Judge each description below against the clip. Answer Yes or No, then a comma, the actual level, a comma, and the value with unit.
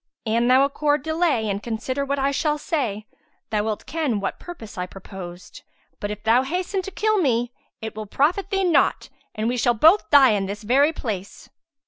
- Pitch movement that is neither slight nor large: No, wide, 6.1 semitones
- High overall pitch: Yes, very high, 250 Hz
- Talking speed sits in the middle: Yes, average, 190 wpm